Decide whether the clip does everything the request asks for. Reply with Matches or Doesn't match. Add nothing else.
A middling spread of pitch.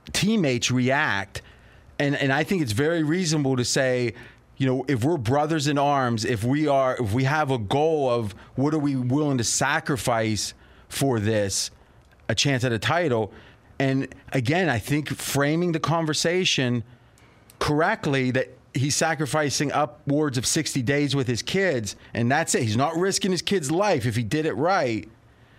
Matches